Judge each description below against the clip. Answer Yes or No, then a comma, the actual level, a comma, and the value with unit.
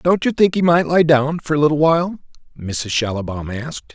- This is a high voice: No, medium, 145 Hz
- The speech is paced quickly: Yes, fast, 215 wpm